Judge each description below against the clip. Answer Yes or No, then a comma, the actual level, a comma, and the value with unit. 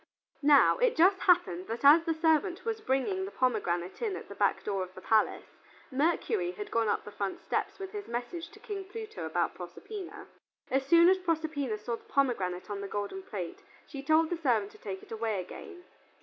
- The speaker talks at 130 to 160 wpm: No, fast, 205 wpm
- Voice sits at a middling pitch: No, very high, 295 Hz